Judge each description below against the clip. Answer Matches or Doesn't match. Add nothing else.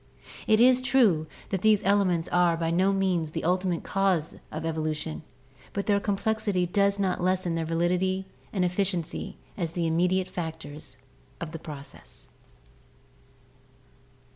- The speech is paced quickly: Doesn't match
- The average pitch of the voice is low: Doesn't match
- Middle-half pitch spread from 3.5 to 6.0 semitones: Doesn't match